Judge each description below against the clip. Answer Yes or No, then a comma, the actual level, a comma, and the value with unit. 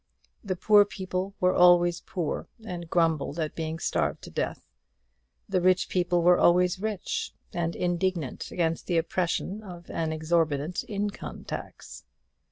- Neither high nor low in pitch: Yes, medium, 175 Hz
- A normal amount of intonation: No, narrow, 1.9 semitones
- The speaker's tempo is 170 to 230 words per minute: No, average, 140 wpm